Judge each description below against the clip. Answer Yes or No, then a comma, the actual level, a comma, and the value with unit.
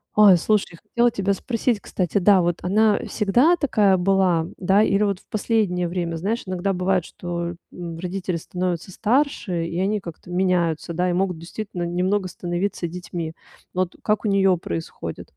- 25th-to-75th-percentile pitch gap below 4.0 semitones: Yes, average, 2.7 semitones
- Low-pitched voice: No, medium, 185 Hz